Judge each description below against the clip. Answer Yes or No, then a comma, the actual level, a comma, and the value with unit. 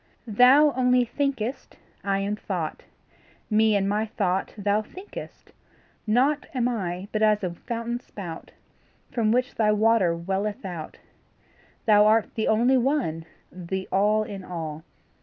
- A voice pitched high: Yes, high, 215 Hz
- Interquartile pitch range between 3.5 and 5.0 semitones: Yes, average, 3.9 semitones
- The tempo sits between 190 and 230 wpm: No, average, 140 wpm